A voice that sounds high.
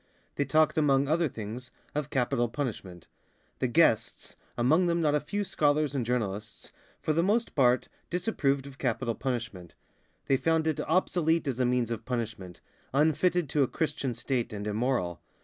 No: low, 135 Hz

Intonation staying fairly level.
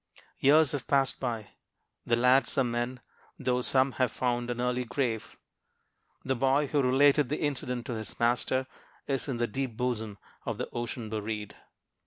Yes: narrow, 2.2 semitones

